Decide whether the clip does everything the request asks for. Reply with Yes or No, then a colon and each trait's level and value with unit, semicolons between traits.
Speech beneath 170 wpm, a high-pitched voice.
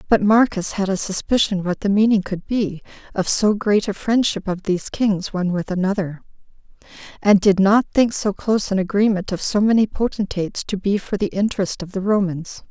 No: average, 195 wpm; high, 200 Hz